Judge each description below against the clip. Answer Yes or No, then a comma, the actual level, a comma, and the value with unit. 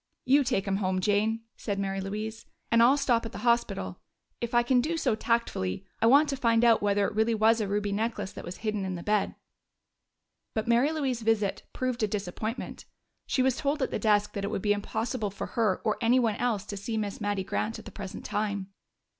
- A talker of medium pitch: No, high, 220 Hz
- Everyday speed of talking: No, fast, 220 wpm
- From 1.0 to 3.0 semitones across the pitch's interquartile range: Yes, average, 2.7 semitones